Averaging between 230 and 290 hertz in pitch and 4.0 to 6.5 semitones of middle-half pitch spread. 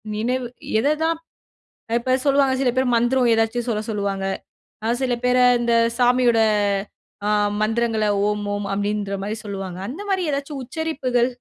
No: high, 235 Hz; average, 3.4 semitones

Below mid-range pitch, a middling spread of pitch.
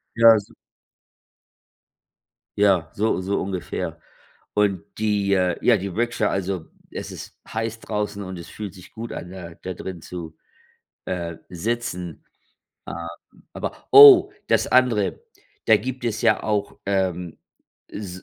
Yes: low, 100 Hz; average, 3.6 semitones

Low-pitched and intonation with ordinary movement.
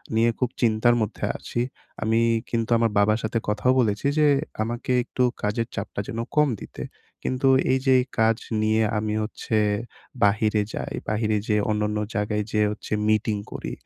No: low, 110 Hz; narrow, 1.8 semitones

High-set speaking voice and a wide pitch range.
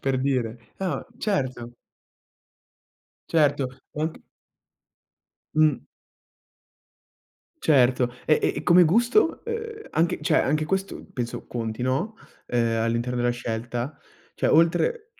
No: medium, 140 Hz; wide, 6.7 semitones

